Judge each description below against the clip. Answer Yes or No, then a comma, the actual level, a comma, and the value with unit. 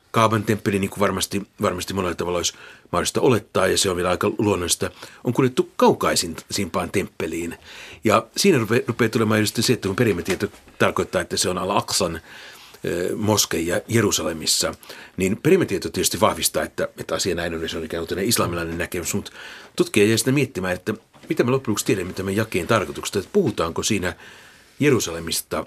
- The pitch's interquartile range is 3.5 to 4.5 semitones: Yes, average, 4.1 semitones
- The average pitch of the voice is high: No, low, 105 Hz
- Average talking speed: No, fast, 170 wpm